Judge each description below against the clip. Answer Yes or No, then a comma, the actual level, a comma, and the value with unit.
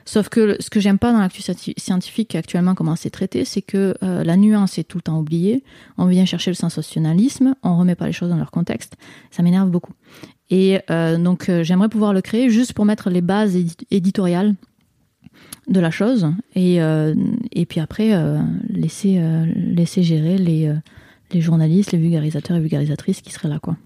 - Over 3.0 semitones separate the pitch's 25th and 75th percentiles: Yes, average, 3.5 semitones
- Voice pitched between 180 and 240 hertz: Yes, medium, 185 Hz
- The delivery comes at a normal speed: Yes, average, 195 wpm